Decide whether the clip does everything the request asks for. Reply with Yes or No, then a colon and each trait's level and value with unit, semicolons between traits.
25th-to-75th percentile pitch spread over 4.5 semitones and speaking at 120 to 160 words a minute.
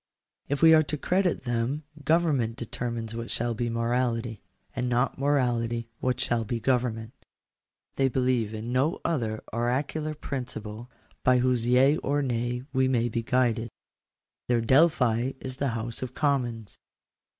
No: narrow, 2.6 semitones; average, 140 wpm